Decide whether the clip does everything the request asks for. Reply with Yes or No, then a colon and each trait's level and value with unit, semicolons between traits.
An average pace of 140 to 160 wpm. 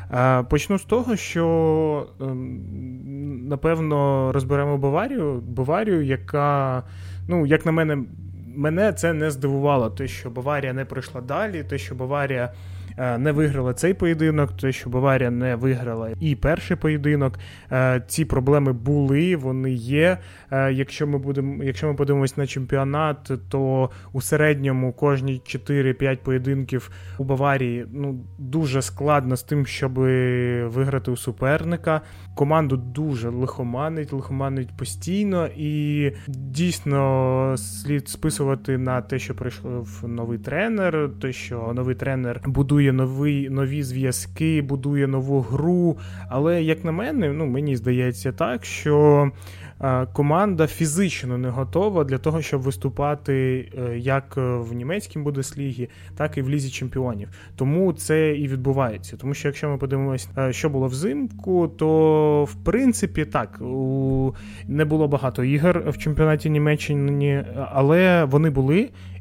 No: average, 125 wpm